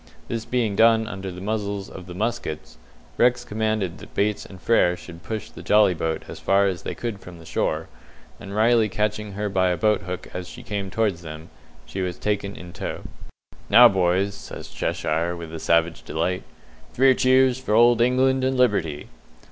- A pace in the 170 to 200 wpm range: Yes, average, 190 wpm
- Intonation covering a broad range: No, average, 4.1 semitones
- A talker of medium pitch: No, low, 100 Hz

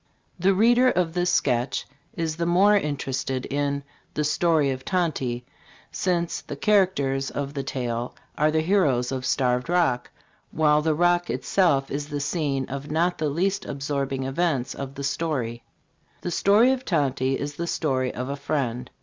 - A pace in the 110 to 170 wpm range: Yes, average, 165 wpm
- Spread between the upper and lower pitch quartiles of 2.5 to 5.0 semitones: Yes, average, 4.4 semitones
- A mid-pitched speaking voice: Yes, medium, 145 Hz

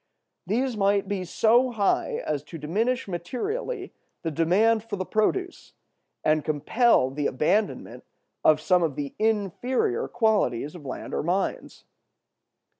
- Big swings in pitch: Yes, wide, 6.9 semitones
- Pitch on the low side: No, high, 200 Hz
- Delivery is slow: Yes, slow, 130 wpm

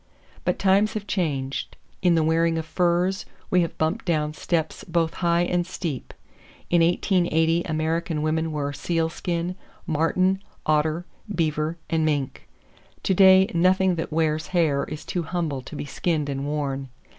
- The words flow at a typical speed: Yes, average, 150 wpm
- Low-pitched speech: No, medium, 165 Hz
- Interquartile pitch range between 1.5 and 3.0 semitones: Yes, narrow, 2.5 semitones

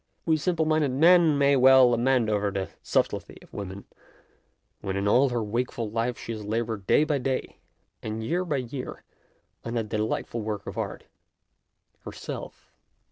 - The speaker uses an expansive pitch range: No, average, 4.6 semitones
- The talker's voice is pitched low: Yes, low, 120 Hz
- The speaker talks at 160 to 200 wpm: Yes, average, 170 wpm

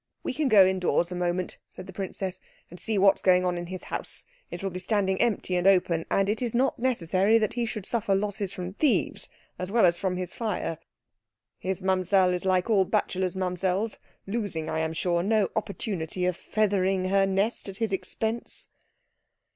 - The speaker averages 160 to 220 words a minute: Yes, average, 190 wpm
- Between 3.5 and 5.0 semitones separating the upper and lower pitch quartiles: No, narrow, 2.6 semitones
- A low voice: No, high, 190 Hz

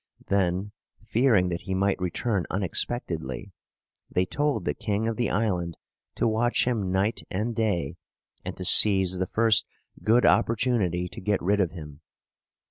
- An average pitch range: Yes, average, 3.9 semitones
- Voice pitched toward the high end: No, low, 100 Hz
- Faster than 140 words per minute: Yes, average, 150 wpm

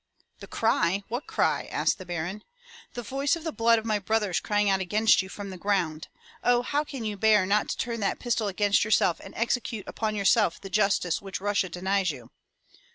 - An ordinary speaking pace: No, fast, 210 wpm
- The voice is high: Yes, high, 205 Hz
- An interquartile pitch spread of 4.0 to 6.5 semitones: No, average, 2.9 semitones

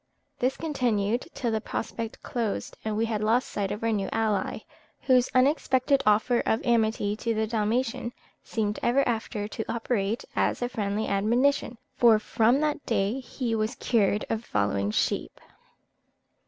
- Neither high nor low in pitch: No, high, 225 Hz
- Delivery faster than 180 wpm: No, average, 155 wpm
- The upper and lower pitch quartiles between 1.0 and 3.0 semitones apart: Yes, average, 2.7 semitones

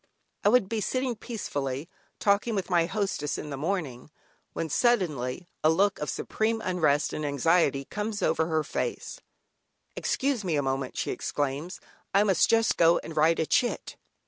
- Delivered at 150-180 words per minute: Yes, average, 165 wpm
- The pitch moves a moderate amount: No, wide, 6.0 semitones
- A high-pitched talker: No, medium, 170 Hz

